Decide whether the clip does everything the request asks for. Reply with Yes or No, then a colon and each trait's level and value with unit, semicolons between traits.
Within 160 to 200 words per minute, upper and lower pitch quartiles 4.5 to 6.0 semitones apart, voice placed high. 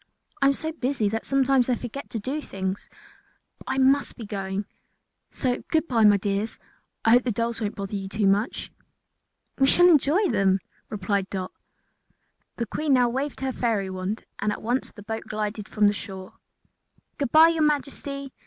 Yes: average, 180 wpm; average, 5.1 semitones; high, 230 Hz